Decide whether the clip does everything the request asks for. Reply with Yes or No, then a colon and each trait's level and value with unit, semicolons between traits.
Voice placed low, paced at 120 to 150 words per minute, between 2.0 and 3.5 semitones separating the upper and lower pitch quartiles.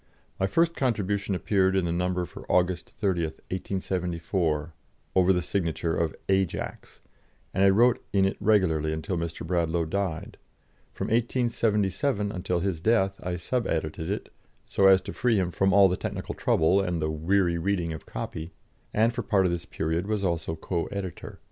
No: very low, 95 Hz; average, 170 wpm; average, 3.0 semitones